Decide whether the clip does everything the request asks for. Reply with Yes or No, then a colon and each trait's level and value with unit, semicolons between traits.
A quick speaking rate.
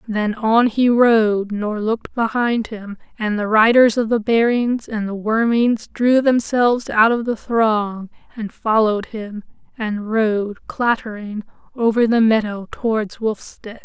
No: average, 145 wpm